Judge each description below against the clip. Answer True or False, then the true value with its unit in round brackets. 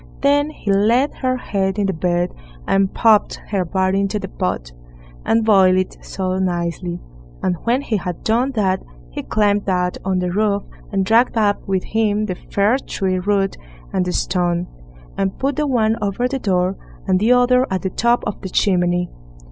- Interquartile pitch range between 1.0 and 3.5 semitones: True (3.2 semitones)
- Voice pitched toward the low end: False (195 Hz)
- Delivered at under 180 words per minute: False (185 wpm)